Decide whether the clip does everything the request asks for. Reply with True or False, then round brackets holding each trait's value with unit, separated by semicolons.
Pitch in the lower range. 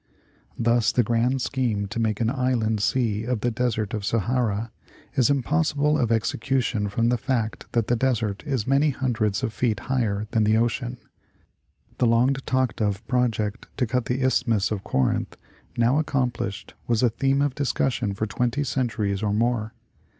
True (120 Hz)